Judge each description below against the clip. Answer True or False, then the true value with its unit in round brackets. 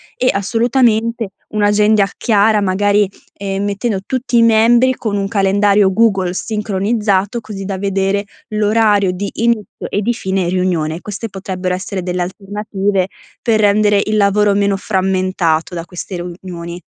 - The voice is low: False (200 Hz)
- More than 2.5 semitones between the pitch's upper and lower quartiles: False (2.2 semitones)